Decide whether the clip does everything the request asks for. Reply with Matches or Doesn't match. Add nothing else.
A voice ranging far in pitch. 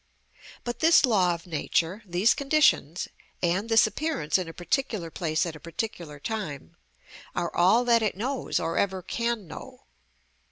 Matches